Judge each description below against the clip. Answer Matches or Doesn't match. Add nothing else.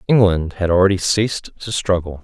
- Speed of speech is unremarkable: Matches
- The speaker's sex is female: Doesn't match